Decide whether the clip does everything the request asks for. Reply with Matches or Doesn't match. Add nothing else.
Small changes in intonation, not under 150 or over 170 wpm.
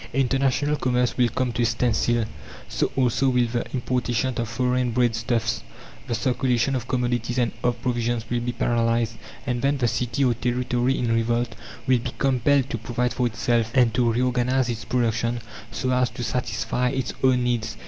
Doesn't match